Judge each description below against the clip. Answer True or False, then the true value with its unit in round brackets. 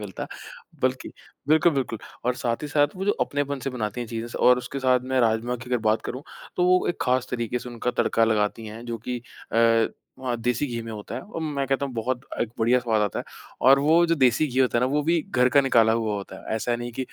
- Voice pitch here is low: True (125 Hz)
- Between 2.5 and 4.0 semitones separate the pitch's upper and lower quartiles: True (3.1 semitones)